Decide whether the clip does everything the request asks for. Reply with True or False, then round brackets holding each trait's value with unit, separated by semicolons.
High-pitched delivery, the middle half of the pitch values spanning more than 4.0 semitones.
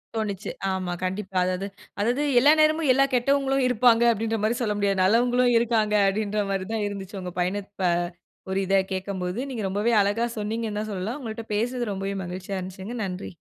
False (210 Hz; 3.7 semitones)